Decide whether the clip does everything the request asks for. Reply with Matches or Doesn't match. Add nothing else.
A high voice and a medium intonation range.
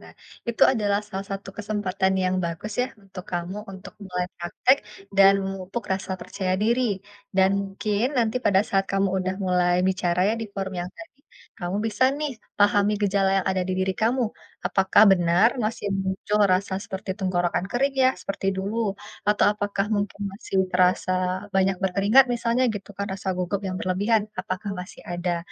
Doesn't match